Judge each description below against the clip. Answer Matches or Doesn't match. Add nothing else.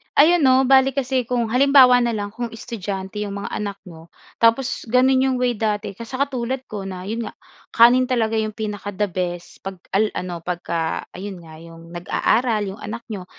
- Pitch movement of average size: Matches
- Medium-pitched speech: Doesn't match